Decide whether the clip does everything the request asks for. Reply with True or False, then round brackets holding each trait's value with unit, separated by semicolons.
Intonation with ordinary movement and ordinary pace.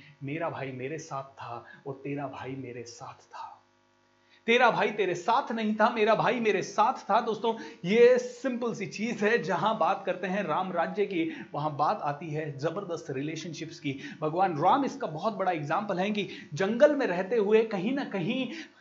False (6.7 semitones; 180 wpm)